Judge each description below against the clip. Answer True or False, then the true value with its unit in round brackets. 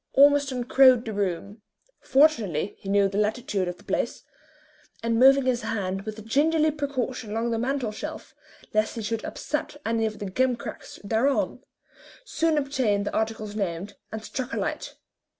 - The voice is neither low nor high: False (225 Hz)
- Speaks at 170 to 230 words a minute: False (160 wpm)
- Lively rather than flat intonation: False (4.3 semitones)